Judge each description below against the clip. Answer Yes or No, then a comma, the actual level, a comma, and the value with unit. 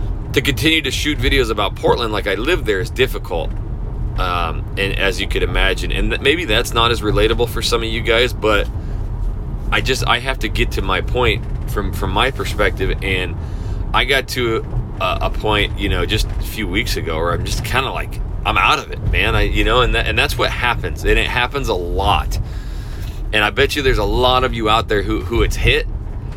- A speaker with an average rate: No, fast, 225 wpm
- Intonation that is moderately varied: Yes, average, 3.1 semitones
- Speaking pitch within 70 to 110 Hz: Yes, low, 105 Hz